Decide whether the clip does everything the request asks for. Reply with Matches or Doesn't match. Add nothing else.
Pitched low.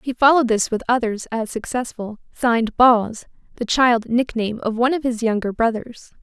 Doesn't match